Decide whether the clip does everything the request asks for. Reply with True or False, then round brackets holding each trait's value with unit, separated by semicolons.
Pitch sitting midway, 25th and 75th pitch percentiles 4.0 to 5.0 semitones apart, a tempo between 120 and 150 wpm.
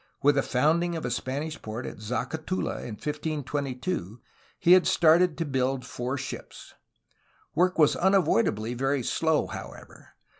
True (145 Hz; 4.4 semitones; 145 wpm)